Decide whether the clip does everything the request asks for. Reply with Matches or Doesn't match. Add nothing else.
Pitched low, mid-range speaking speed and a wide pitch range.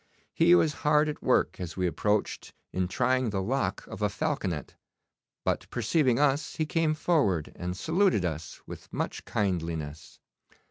Matches